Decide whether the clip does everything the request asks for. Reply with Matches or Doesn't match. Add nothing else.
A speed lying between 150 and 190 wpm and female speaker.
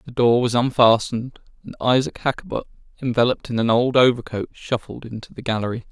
Doesn't match